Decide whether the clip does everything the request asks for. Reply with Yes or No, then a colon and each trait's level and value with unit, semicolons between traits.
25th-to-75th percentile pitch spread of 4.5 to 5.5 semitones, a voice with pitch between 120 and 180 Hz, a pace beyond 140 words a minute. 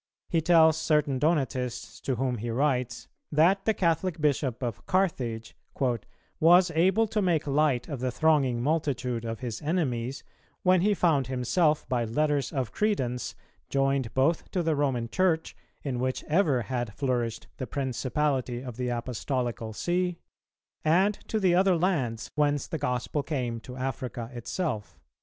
Yes: average, 4.8 semitones; low, 135 Hz; average, 150 wpm